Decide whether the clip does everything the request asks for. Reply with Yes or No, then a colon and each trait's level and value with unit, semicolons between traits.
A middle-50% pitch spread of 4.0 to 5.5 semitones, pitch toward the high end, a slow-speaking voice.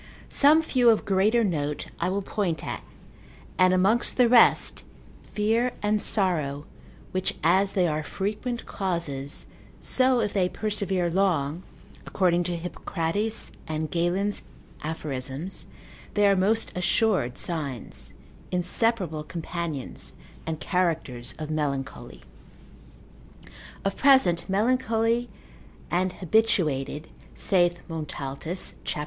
No: average, 4.9 semitones; medium, 180 Hz; slow, 105 wpm